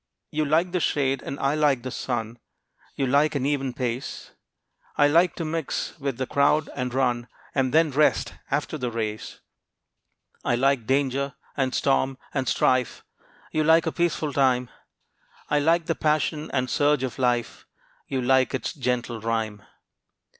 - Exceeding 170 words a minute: No, average, 160 wpm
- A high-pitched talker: No, low, 135 Hz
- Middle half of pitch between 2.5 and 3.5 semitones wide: Yes, average, 3.0 semitones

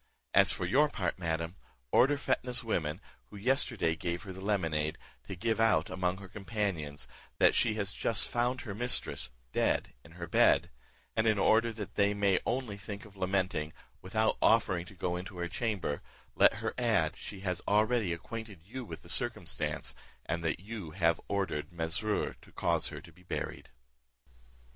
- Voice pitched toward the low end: Yes, low, 100 Hz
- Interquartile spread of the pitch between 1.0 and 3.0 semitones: No, average, 4.3 semitones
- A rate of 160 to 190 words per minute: Yes, average, 170 wpm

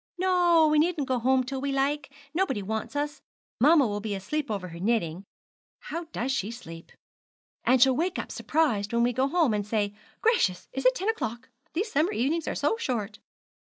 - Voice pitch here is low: No, very high, 265 Hz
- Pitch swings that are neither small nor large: No, wide, 6.4 semitones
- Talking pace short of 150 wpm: No, average, 190 wpm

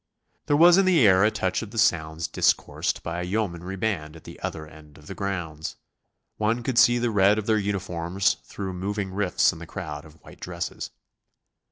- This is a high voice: No, very low, 95 Hz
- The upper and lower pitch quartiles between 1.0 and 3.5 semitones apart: No, average, 4.5 semitones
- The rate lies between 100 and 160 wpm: No, average, 200 wpm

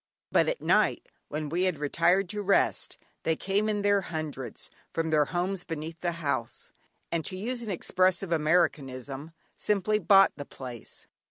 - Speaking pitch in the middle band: Yes, medium, 170 Hz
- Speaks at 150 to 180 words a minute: Yes, average, 160 wpm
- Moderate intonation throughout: Yes, average, 4.2 semitones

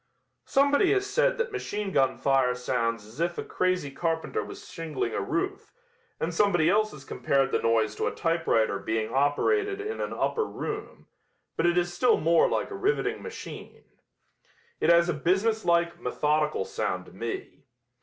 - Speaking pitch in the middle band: Yes, medium, 170 Hz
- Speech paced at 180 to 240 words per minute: No, average, 170 wpm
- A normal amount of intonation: No, wide, 8.3 semitones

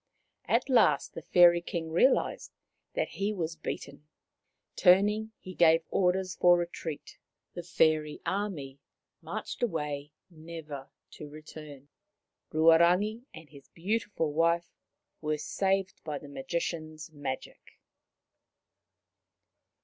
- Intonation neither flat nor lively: Yes, average, 3.4 semitones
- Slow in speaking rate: Yes, slow, 105 wpm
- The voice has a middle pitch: Yes, medium, 165 Hz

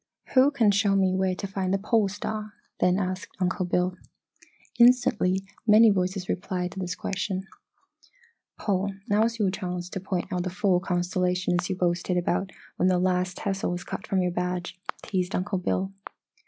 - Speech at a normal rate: Yes, average, 170 wpm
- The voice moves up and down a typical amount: No, narrow, 1.7 semitones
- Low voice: No, medium, 185 Hz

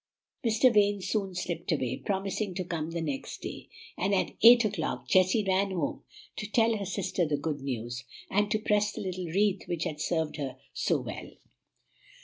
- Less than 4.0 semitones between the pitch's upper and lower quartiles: No, average, 4.4 semitones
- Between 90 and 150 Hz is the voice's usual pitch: No, medium, 185 Hz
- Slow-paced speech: No, average, 180 wpm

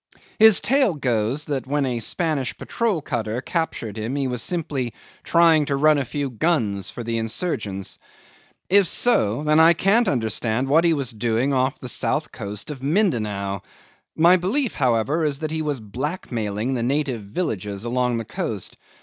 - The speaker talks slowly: No, average, 165 wpm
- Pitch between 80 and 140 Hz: Yes, low, 135 Hz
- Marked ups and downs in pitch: Yes, wide, 5.9 semitones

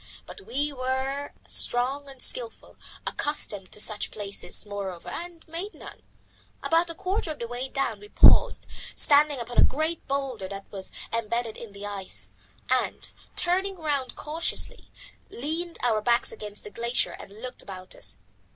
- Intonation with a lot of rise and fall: Yes, wide, 6.9 semitones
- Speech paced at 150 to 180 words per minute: Yes, average, 155 wpm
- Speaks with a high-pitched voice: Yes, very high, 260 Hz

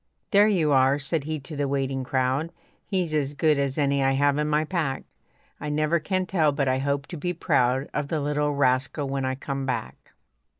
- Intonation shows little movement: Yes, narrow, 2.3 semitones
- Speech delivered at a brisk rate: Yes, fast, 210 wpm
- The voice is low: No, medium, 145 Hz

